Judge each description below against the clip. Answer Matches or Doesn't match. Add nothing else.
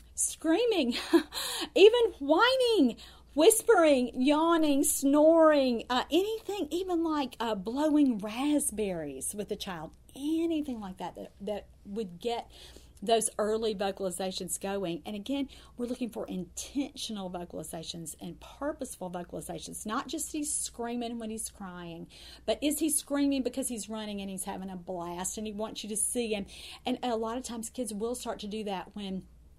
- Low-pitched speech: Doesn't match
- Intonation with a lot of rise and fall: Matches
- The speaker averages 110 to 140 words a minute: Doesn't match